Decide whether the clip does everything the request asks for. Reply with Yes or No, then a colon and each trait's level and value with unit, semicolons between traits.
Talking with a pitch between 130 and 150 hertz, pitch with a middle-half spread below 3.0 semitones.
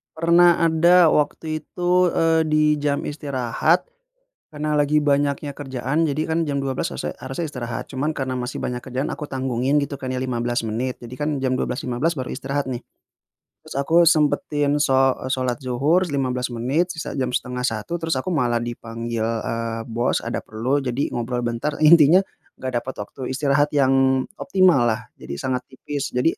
No: low, 135 Hz; average, 3.5 semitones